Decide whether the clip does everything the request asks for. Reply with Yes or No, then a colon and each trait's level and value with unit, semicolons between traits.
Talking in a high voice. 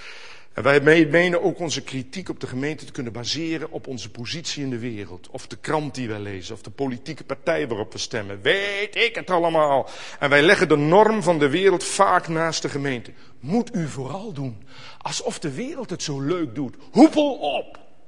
No: medium, 150 Hz